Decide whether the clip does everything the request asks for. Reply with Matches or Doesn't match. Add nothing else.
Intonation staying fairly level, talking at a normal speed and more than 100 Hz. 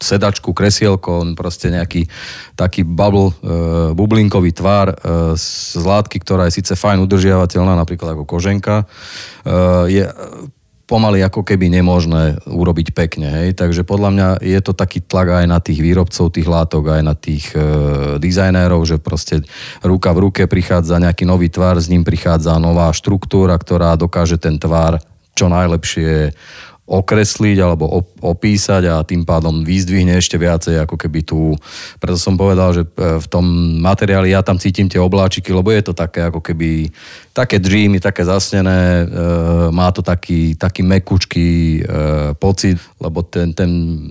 Doesn't match